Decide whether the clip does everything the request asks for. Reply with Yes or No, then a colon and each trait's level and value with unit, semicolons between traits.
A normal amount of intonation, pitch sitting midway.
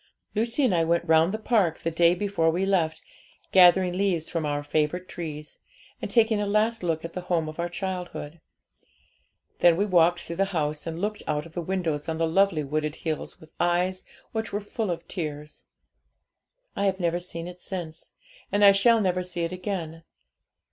Yes: average, 3.1 semitones; medium, 175 Hz